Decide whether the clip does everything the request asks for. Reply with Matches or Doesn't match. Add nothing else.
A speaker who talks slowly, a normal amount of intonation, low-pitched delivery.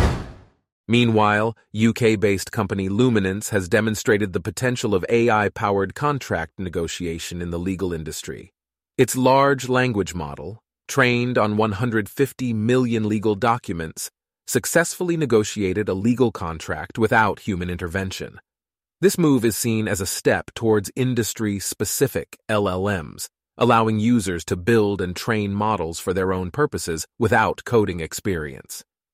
Matches